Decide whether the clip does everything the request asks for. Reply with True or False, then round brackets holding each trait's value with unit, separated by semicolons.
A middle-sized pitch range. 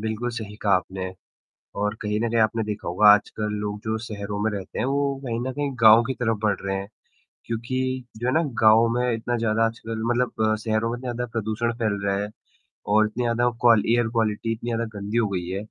False (2.2 semitones)